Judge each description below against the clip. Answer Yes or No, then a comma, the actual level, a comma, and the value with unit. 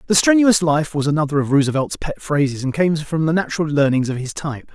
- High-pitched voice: No, medium, 155 Hz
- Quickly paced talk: Yes, fast, 225 wpm